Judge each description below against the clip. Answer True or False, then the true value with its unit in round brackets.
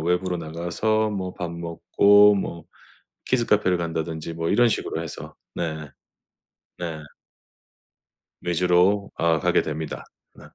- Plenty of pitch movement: False (3.3 semitones)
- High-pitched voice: False (85 Hz)